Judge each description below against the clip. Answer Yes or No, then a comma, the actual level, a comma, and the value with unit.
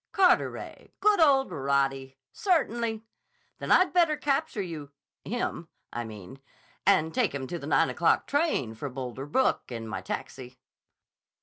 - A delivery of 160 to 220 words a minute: No, slow, 135 wpm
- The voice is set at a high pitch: No, medium, 160 Hz